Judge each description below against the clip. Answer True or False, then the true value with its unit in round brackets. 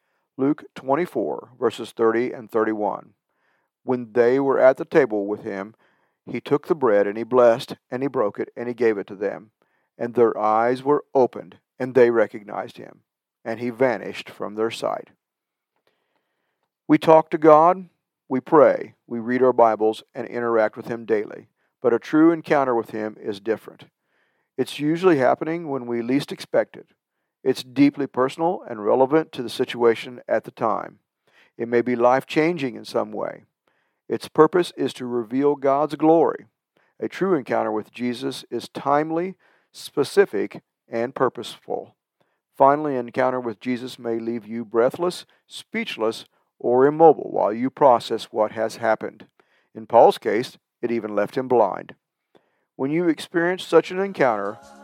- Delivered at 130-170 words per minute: True (160 wpm)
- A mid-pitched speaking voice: False (125 Hz)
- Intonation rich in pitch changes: False (4.8 semitones)